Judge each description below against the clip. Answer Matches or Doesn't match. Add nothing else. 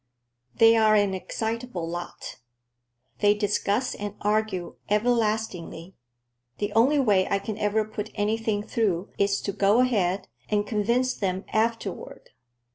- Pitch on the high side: Matches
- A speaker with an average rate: Doesn't match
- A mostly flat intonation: Matches